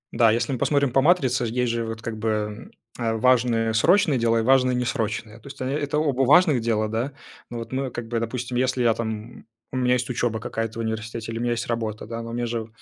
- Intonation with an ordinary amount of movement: No, narrow, 2.2 semitones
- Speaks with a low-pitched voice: Yes, low, 120 Hz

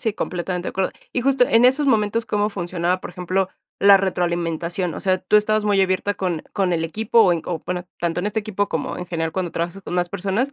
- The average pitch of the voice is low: No, high, 190 Hz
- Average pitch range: Yes, average, 3.1 semitones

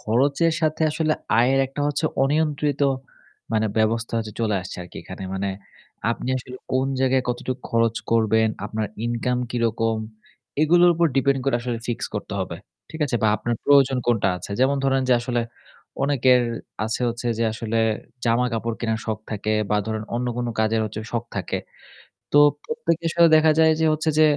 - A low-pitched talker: Yes, low, 120 Hz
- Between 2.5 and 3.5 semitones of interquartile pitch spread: No, average, 4.0 semitones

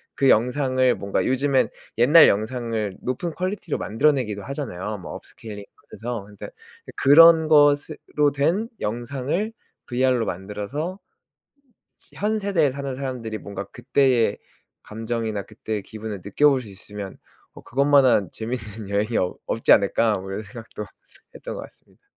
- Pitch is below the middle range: Yes, low, 120 Hz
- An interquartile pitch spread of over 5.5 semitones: No, average, 5.1 semitones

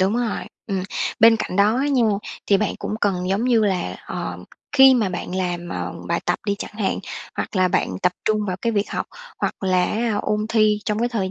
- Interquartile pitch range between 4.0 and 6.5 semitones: No, average, 3.3 semitones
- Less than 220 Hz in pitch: Yes, high, 210 Hz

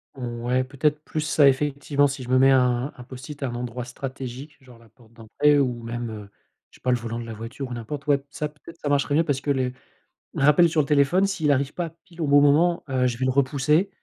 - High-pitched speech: No, low, 135 Hz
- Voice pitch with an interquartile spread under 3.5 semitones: Yes, average, 3.0 semitones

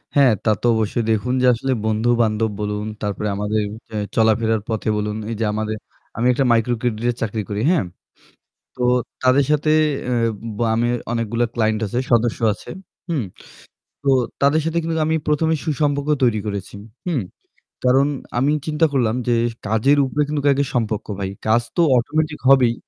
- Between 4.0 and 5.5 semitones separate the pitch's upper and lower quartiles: Yes, average, 4.3 semitones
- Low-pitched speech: Yes, low, 120 Hz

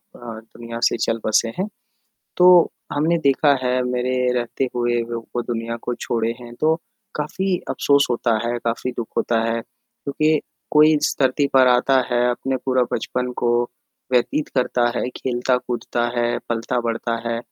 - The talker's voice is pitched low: Yes, low, 125 Hz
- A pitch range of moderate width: No, narrow, 2.2 semitones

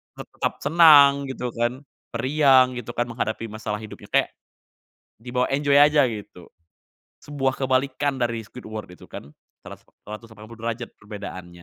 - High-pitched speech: No, low, 120 Hz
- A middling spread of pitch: Yes, average, 4.2 semitones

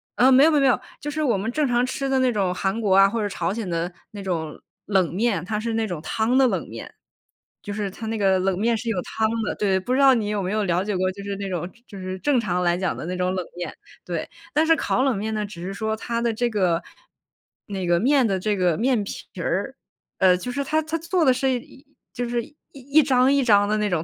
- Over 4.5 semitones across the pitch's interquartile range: Yes, average, 5.0 semitones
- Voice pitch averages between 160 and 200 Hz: No, high, 215 Hz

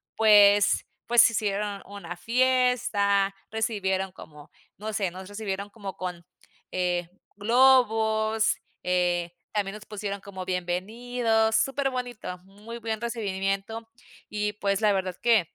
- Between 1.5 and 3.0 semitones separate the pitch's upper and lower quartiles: Yes, narrow, 2.6 semitones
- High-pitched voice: Yes, high, 205 Hz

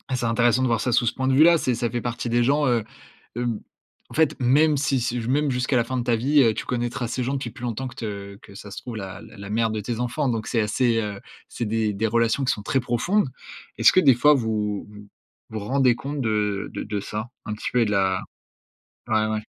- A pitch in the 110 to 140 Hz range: Yes, low, 120 Hz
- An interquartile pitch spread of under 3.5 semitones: Yes, average, 3.1 semitones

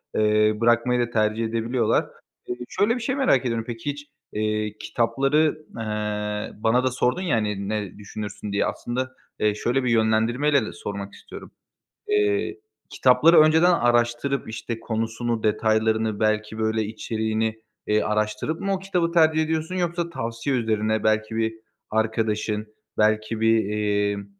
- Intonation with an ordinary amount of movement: Yes, average, 3.8 semitones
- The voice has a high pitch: No, low, 115 Hz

